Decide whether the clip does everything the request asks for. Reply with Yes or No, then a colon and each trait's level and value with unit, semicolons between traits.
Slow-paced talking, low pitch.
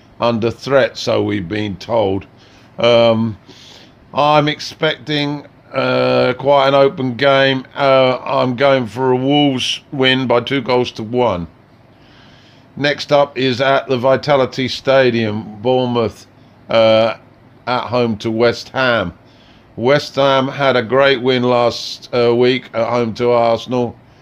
Yes: slow, 130 wpm; low, 125 Hz